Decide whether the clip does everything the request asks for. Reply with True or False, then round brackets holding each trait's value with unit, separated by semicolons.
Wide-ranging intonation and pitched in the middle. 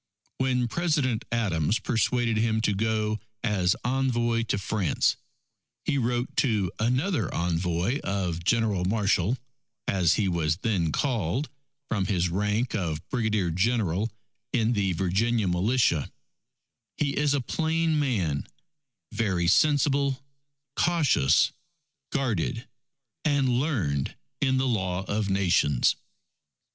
False (5.7 semitones; 110 Hz)